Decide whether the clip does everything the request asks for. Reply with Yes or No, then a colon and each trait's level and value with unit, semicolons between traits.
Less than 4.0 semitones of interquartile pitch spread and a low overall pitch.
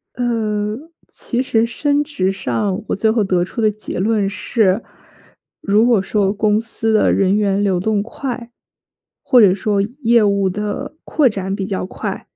No: narrow, 2.6 semitones; high, 210 Hz